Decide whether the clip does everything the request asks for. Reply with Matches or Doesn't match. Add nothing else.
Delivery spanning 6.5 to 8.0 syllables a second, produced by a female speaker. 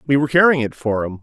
Doesn't match